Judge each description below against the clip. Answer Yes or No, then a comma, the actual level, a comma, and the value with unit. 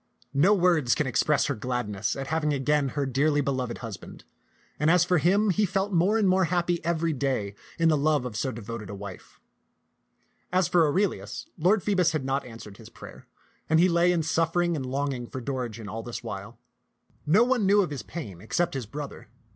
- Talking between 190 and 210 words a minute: Yes, average, 200 wpm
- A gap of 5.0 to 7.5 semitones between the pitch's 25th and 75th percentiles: Yes, wide, 5.6 semitones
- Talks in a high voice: No, medium, 150 Hz